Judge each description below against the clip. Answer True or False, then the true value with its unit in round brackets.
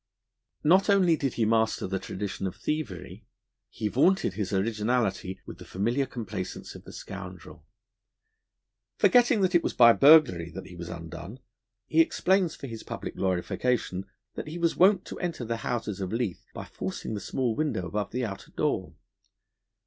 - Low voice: True (115 Hz)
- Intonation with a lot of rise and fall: True (8.2 semitones)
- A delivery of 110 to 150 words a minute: False (165 wpm)